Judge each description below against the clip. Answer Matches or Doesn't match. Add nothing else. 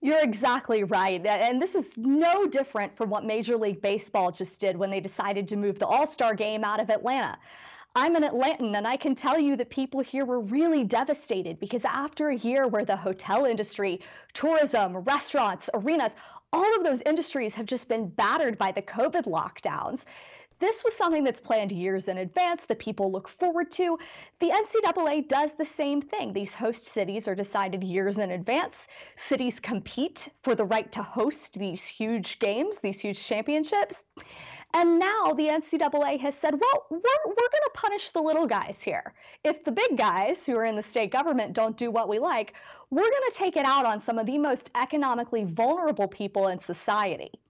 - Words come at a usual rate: Matches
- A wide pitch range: Matches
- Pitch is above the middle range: Matches